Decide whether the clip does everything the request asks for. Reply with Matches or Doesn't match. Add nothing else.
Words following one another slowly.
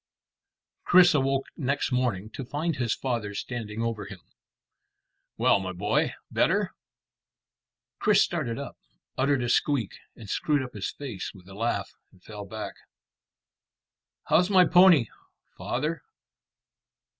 Matches